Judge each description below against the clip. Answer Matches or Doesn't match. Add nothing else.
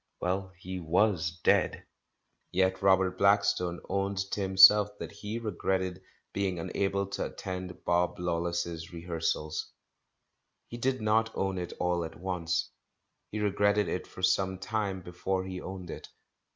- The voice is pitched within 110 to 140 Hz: Doesn't match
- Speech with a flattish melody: Matches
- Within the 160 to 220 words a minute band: Doesn't match